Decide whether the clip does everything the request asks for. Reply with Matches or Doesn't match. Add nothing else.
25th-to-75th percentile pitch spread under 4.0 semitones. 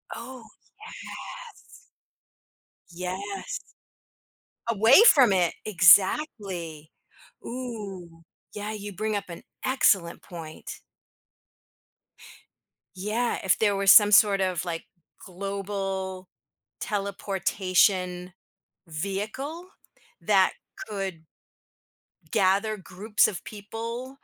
Matches